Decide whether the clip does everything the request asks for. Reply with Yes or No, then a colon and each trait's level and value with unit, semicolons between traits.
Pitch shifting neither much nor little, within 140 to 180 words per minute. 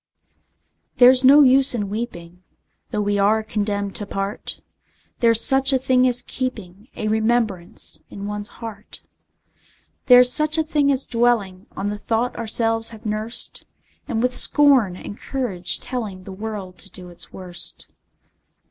Yes: average, 3.7 semitones; average, 150 wpm